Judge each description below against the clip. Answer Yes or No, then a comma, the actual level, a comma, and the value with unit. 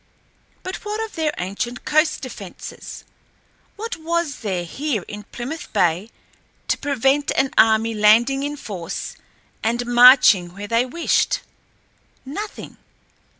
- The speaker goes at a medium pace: No, slow, 120 wpm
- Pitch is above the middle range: Yes, high, 245 Hz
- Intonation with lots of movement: Yes, wide, 6.0 semitones